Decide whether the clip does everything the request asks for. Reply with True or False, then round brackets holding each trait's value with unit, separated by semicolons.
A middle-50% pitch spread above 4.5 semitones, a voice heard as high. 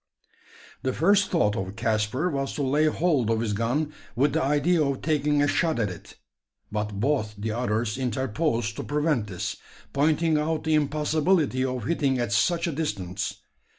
False (5.4 semitones; 135 Hz)